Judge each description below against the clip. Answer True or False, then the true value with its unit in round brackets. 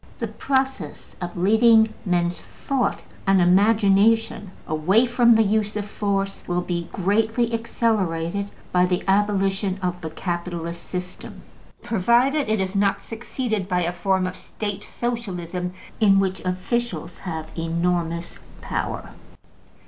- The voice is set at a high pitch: True (195 Hz)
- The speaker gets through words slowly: True (125 wpm)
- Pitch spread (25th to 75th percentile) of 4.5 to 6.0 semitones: False (3.7 semitones)